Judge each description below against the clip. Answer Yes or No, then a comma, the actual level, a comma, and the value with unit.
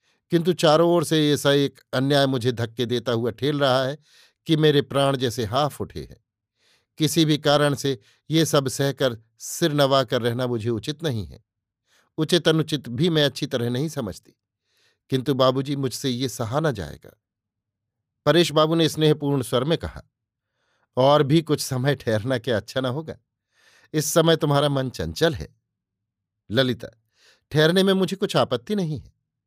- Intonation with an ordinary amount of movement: Yes, average, 4.2 semitones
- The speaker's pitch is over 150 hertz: No, low, 135 Hz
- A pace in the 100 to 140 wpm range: No, average, 165 wpm